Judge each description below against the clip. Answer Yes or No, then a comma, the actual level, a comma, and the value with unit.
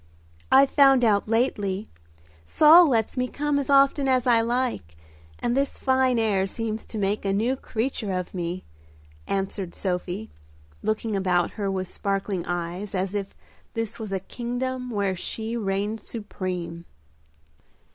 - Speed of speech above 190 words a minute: No, average, 145 wpm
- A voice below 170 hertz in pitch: No, high, 215 Hz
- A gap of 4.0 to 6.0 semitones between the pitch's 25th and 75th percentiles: Yes, average, 4.6 semitones